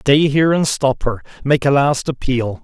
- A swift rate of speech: No, average, 180 wpm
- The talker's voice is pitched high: No, low, 135 Hz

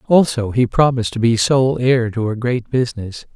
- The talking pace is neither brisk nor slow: Yes, average, 195 wpm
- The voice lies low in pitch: Yes, low, 120 Hz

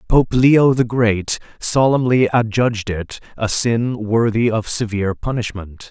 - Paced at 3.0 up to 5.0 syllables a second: Yes, 4.1 syllables/s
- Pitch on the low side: Yes, low, 115 Hz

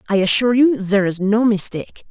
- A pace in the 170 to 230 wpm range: Yes, average, 200 wpm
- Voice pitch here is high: Yes, high, 210 Hz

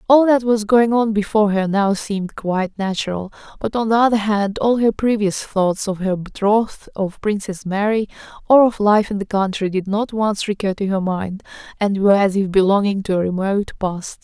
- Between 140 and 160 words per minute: No, average, 200 wpm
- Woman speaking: Yes, female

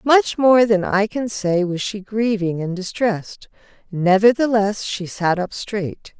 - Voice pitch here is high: Yes, high, 205 Hz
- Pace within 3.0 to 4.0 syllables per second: Yes, 3.9 syllables/s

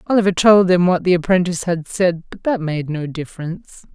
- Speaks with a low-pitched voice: No, medium, 175 Hz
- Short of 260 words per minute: Yes, average, 200 wpm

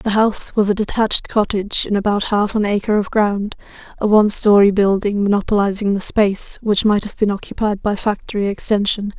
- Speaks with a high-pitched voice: Yes, high, 205 Hz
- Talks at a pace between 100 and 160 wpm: No, average, 185 wpm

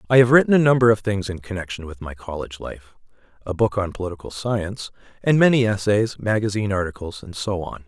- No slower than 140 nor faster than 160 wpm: No, average, 190 wpm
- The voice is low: Yes, low, 100 Hz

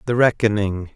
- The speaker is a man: Yes, male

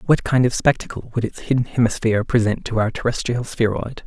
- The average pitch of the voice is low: Yes, low, 120 Hz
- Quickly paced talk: No, average, 190 wpm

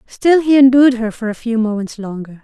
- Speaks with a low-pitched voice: No, high, 235 Hz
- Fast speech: Yes, fast, 220 wpm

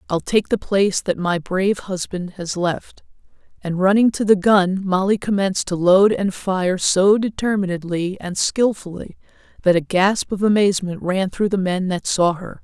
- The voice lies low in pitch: No, high, 190 Hz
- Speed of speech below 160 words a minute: No, average, 175 wpm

